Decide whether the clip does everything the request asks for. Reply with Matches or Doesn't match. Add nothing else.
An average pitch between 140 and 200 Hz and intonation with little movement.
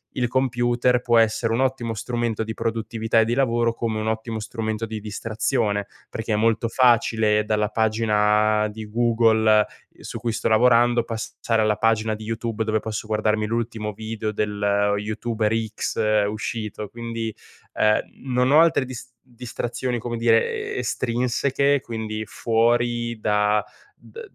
Doesn't match